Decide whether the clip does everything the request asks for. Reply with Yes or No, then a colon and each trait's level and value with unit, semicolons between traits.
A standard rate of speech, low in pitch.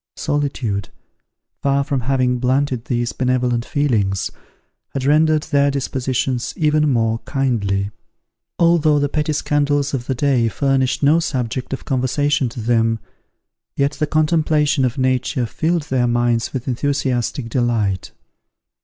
No: slow, 125 wpm; low, 130 Hz